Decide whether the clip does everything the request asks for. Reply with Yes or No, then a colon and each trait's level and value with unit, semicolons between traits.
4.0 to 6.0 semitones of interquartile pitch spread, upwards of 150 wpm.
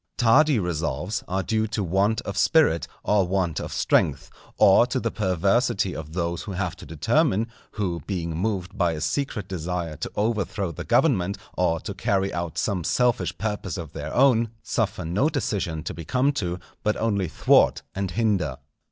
Yes: average, 4.4 semitones; average, 175 wpm